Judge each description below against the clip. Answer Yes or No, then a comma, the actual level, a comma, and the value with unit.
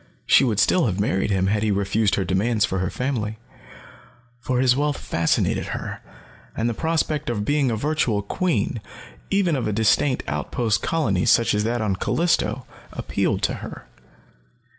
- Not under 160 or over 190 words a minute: Yes, average, 165 wpm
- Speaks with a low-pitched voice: Yes, low, 110 Hz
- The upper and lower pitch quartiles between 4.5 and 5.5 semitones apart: Yes, average, 5.2 semitones